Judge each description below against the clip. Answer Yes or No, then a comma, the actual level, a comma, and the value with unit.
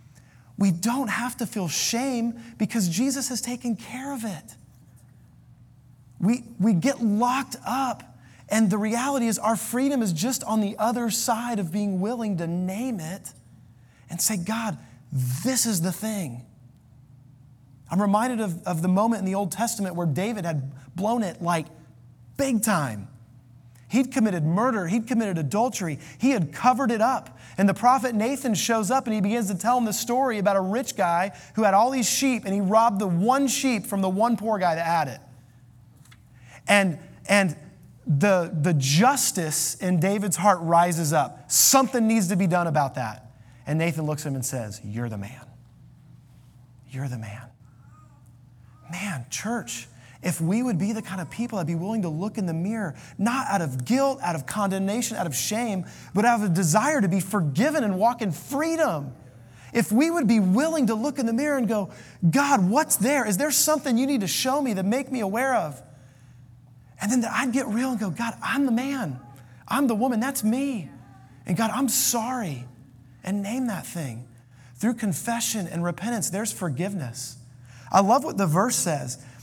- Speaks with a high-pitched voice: Yes, high, 195 Hz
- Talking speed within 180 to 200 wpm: Yes, average, 185 wpm